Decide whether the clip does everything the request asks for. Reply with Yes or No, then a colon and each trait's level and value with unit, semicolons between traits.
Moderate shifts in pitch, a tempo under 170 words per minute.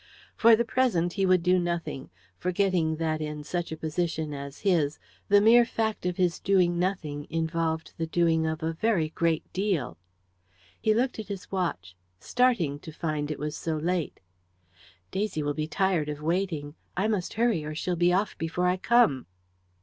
No: average, 3.7 semitones; average, 175 wpm